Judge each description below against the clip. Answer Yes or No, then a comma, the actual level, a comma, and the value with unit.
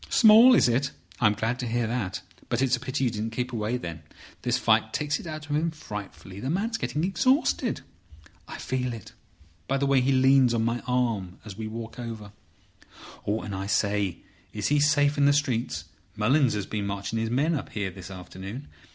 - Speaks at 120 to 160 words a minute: No, average, 200 wpm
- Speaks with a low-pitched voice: Yes, low, 120 Hz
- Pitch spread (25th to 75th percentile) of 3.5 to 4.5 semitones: No, average, 5.2 semitones